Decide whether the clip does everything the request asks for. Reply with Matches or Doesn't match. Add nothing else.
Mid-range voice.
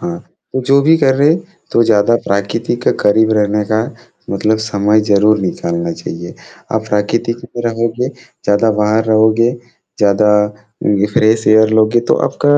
Doesn't match